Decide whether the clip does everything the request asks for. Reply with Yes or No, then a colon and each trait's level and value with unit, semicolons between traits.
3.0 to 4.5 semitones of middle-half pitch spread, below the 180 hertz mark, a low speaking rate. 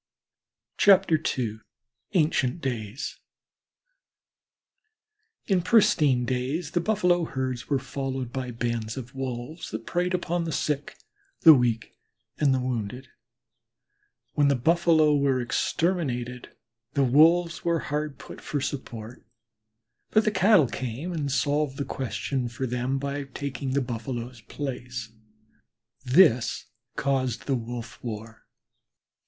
Yes: average, 4.1 semitones; low, 135 Hz; slow, 115 wpm